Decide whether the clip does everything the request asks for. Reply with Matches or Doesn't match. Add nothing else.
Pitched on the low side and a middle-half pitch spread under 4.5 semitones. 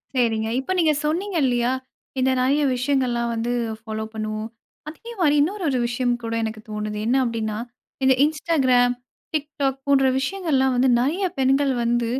Doesn't match